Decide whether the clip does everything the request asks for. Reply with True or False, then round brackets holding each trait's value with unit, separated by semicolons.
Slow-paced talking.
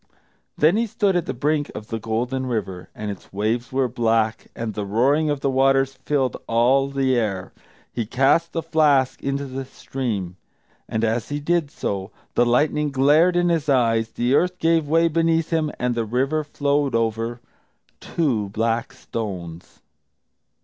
False (170 wpm)